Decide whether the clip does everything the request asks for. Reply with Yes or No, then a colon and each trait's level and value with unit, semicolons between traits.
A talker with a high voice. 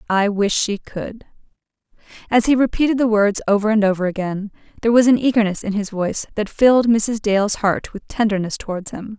Yes: high, 210 Hz